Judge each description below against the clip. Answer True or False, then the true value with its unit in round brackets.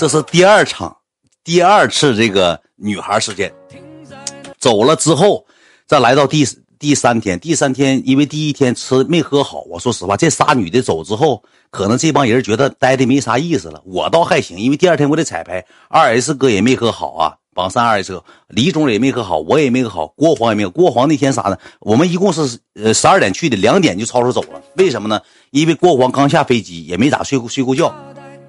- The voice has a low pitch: True (130 Hz)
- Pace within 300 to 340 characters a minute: True (310 characters per minute)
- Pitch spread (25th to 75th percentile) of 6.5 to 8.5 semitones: False (5.1 semitones)